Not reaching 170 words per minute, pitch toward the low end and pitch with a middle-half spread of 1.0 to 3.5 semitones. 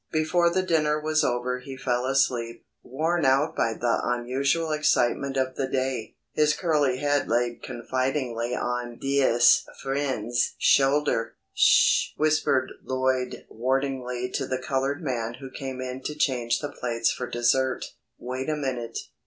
Yes: average, 145 wpm; low, 130 Hz; average, 2.8 semitones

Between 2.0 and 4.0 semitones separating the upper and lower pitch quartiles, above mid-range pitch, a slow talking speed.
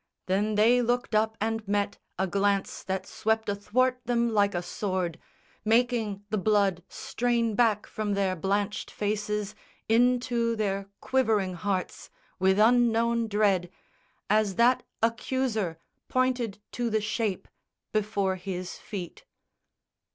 Yes: average, 2.9 semitones; high, 210 Hz; slow, 120 wpm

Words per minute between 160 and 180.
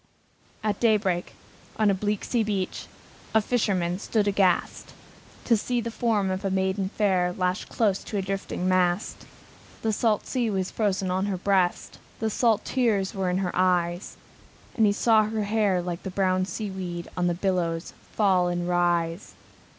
Yes: average, 165 wpm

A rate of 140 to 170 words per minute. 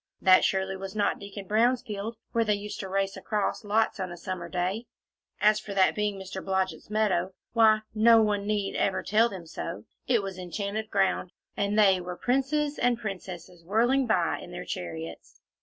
No: average, 190 wpm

